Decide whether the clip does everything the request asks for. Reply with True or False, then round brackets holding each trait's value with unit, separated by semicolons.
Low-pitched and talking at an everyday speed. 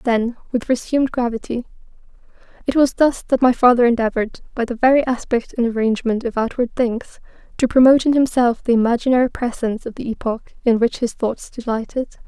False (240 Hz; 165 wpm)